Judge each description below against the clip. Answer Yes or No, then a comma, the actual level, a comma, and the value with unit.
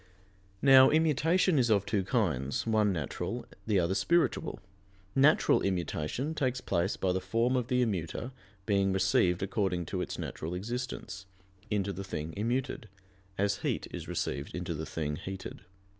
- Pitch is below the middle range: Yes, low, 100 Hz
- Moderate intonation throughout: No, wide, 5.7 semitones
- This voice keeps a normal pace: Yes, average, 150 wpm